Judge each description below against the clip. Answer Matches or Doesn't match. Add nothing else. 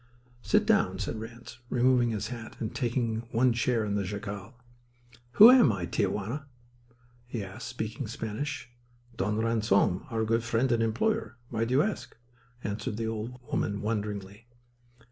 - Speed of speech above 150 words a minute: Matches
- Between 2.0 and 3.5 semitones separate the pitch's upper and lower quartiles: Matches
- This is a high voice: Doesn't match